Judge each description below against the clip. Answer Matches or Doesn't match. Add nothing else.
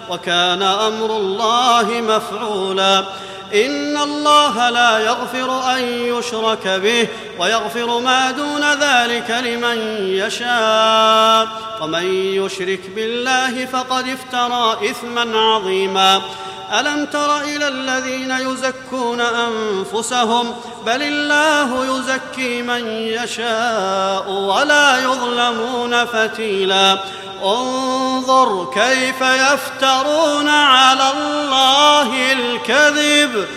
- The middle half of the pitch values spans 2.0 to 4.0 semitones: Matches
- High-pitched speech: Matches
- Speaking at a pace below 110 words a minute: Matches